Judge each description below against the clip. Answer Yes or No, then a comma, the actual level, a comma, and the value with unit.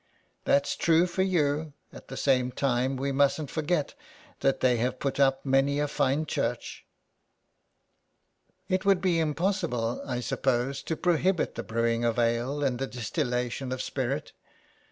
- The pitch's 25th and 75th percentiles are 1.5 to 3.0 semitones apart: No, average, 4.1 semitones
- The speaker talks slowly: No, average, 155 wpm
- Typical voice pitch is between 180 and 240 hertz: No, low, 135 Hz